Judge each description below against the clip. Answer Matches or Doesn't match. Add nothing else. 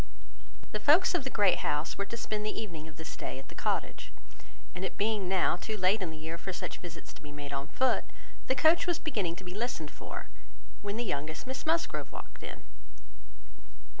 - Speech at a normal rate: Doesn't match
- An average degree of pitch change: Doesn't match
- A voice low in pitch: Doesn't match